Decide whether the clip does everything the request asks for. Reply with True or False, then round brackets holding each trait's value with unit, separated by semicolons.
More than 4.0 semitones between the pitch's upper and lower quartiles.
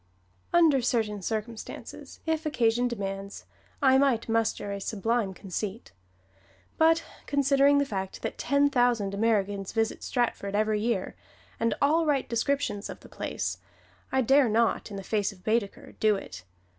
True (4.9 semitones)